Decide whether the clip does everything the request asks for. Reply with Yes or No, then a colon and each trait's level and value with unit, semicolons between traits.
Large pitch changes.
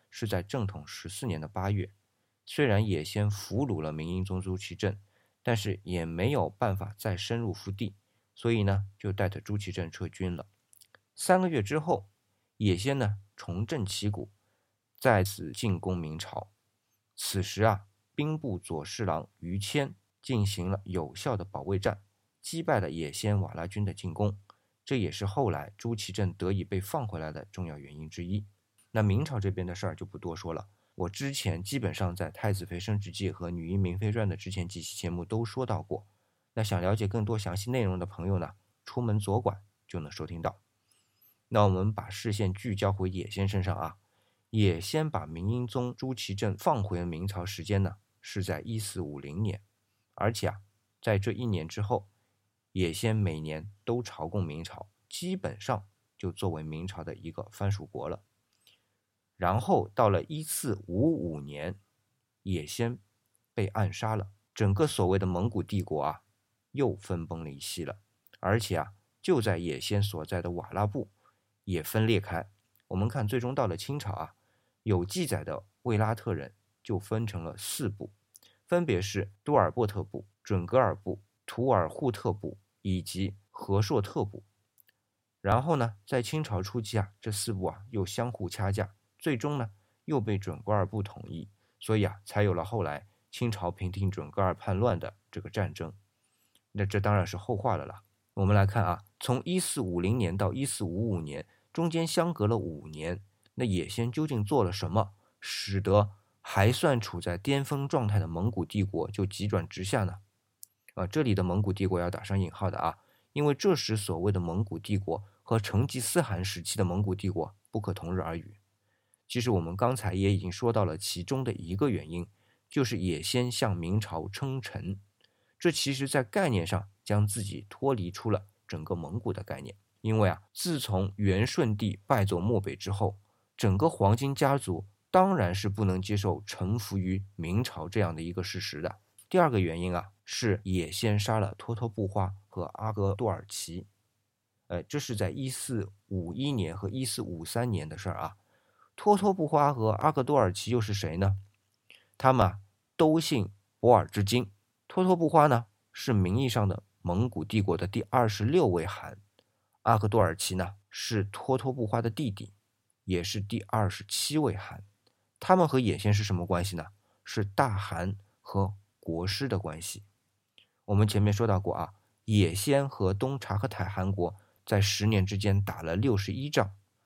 No: average, 3.3 semitones